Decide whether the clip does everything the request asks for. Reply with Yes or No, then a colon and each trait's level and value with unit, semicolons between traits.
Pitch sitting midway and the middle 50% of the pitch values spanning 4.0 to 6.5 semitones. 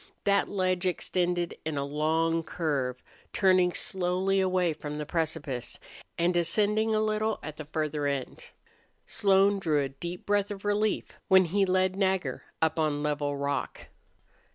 Yes: medium, 175 Hz; average, 4.3 semitones